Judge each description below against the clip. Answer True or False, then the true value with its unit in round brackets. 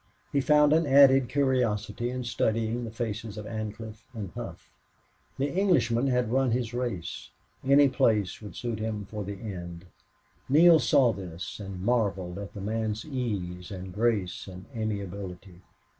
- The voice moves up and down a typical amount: True (4.1 semitones)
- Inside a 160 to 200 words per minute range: False (150 wpm)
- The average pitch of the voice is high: False (110 Hz)